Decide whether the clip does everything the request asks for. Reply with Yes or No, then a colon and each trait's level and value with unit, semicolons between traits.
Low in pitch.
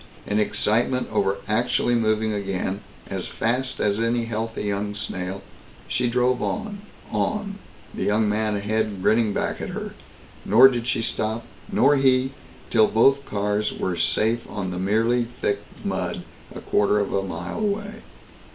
Yes: low, 110 Hz